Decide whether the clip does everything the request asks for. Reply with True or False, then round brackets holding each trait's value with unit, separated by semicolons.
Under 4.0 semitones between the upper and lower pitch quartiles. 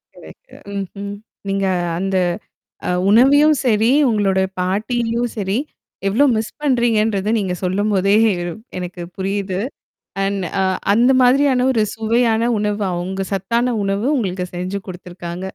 True (3.5 semitones)